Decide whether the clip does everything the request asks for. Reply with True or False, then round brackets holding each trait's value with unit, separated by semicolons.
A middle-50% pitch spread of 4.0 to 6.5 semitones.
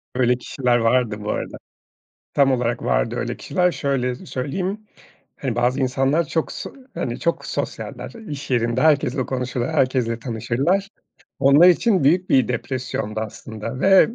False (3.4 semitones)